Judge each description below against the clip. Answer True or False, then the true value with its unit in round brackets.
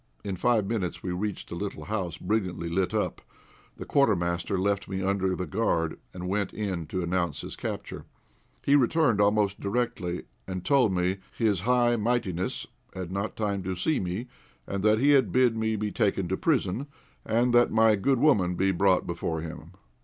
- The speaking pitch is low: True (100 Hz)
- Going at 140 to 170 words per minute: False (180 wpm)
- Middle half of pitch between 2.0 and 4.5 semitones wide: True (3.7 semitones)